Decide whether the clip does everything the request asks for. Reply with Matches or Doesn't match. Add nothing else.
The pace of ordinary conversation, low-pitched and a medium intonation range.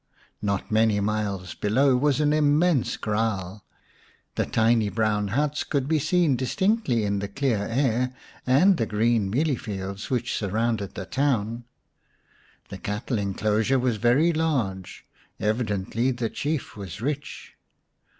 Doesn't match